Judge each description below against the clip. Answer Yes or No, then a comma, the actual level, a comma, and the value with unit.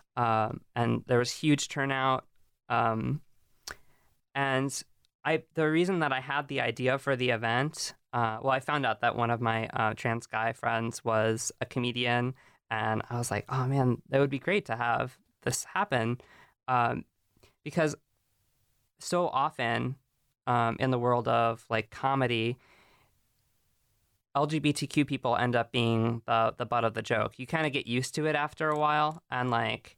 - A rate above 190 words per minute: No, average, 165 wpm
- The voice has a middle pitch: No, low, 125 Hz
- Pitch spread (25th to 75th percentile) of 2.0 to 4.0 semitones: Yes, average, 3.2 semitones